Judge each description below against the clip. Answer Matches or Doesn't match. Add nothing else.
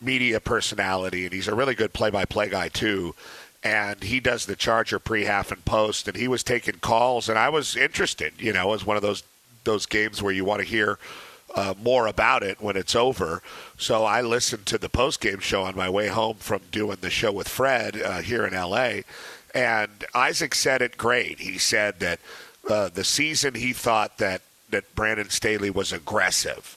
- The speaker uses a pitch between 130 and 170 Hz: Doesn't match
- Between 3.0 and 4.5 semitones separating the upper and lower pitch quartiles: Doesn't match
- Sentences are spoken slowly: Doesn't match